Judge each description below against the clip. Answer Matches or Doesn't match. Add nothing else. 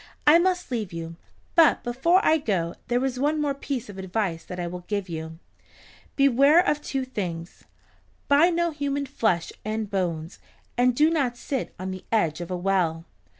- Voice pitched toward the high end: Matches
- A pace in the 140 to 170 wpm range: Doesn't match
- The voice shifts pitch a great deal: Matches